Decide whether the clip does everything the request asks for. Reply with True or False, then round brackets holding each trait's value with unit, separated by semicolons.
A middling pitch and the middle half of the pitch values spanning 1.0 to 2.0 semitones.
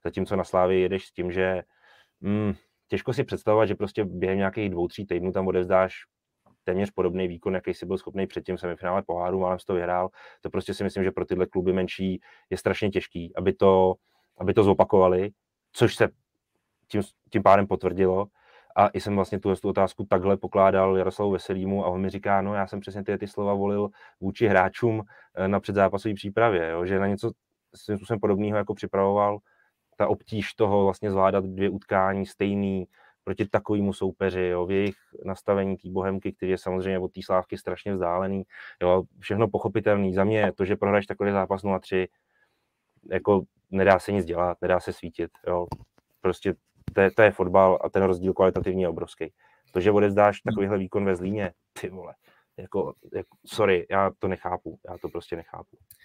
False (95 Hz; 1.4 semitones)